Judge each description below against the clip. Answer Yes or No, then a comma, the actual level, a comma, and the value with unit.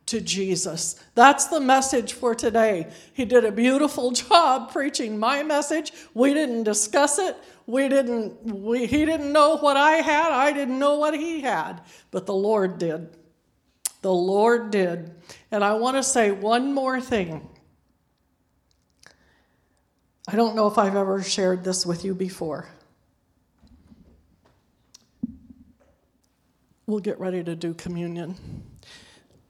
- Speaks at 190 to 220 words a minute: No, slow, 135 wpm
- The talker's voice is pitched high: Yes, high, 230 Hz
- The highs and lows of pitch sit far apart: Yes, wide, 6.3 semitones